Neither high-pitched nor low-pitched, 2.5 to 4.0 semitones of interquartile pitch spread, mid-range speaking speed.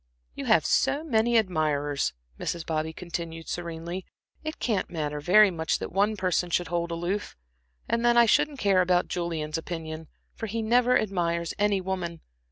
No: medium, 175 Hz; average, 4.6 semitones; average, 165 wpm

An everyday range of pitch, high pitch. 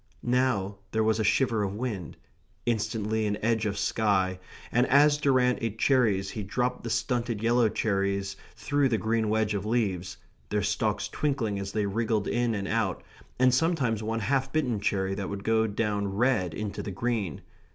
No: average, 3.4 semitones; low, 110 Hz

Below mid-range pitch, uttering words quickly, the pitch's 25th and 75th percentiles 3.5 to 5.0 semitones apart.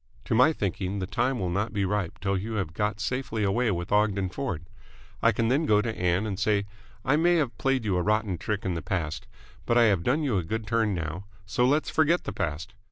Yes: low, 105 Hz; fast, 235 wpm; average, 4.2 semitones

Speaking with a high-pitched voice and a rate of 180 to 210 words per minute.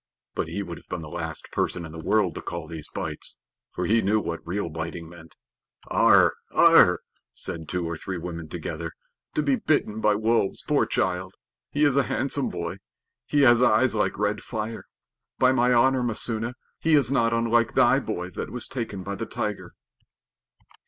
No: low, 105 Hz; average, 185 wpm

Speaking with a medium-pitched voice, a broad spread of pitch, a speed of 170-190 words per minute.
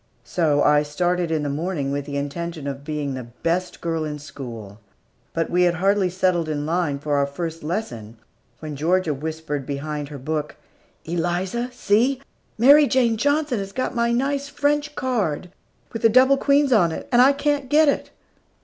Yes: medium, 170 Hz; wide, 8.2 semitones; average, 175 wpm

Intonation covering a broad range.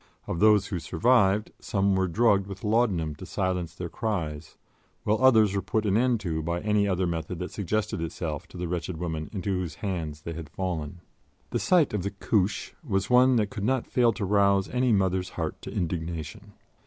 No: average, 3.9 semitones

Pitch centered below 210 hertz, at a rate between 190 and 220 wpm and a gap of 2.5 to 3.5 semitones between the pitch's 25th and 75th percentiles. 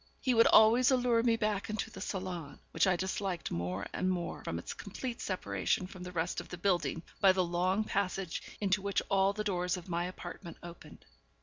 Yes: medium, 185 Hz; average, 200 wpm; average, 2.8 semitones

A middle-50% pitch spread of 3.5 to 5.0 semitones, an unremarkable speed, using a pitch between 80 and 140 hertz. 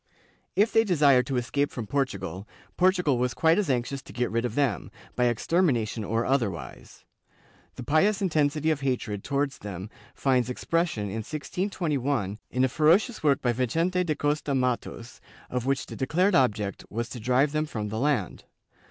Yes: average, 4.6 semitones; average, 170 wpm; low, 135 Hz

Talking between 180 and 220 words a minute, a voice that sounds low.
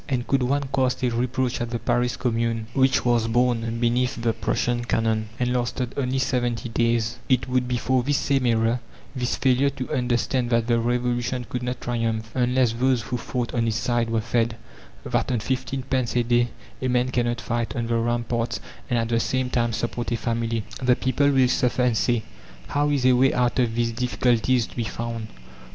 Yes: average, 200 wpm; low, 120 Hz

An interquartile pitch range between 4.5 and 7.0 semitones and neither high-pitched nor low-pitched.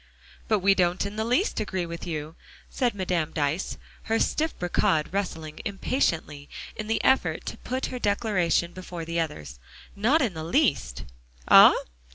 Yes: average, 5.1 semitones; medium, 180 Hz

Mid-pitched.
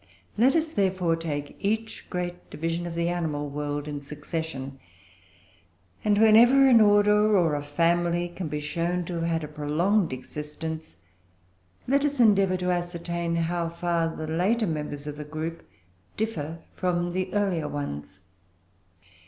Yes: medium, 170 Hz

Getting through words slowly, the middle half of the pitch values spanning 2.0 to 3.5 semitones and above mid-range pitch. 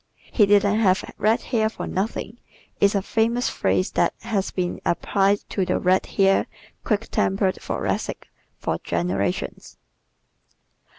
Yes: slow, 130 wpm; average, 2.7 semitones; high, 200 Hz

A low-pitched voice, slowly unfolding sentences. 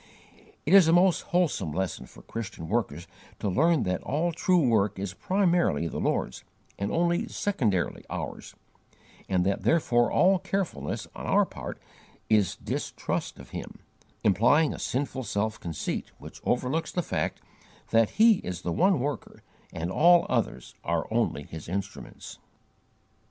No: low, 120 Hz; average, 145 wpm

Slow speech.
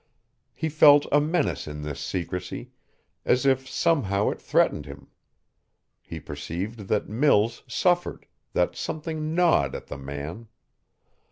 Yes: slow, 125 wpm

